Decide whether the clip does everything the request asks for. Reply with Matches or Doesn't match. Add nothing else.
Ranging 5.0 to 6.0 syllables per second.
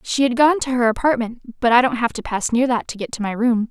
Matches